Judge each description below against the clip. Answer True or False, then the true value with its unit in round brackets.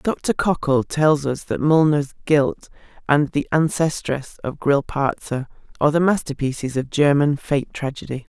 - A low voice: False (145 Hz)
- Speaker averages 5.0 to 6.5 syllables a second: False (4.4 syllables/s)